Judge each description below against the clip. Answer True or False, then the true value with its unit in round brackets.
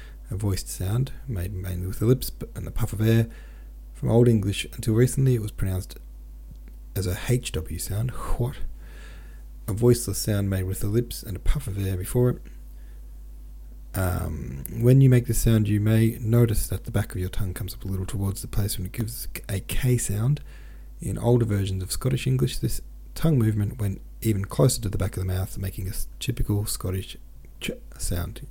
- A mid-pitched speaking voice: False (100 Hz)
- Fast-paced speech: False (195 wpm)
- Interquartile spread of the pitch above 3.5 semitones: True (4.5 semitones)